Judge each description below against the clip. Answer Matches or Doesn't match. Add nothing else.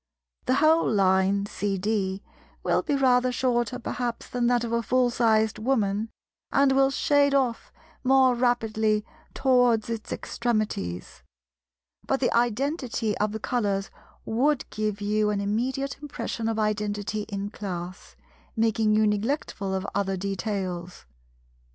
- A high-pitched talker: Matches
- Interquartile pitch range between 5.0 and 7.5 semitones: Doesn't match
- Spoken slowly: Matches